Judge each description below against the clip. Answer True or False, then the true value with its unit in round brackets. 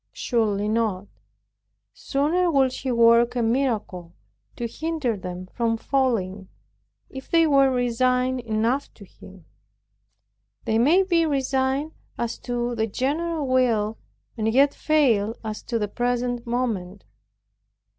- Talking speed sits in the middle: False (125 wpm)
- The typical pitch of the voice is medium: False (245 Hz)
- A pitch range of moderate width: True (3.5 semitones)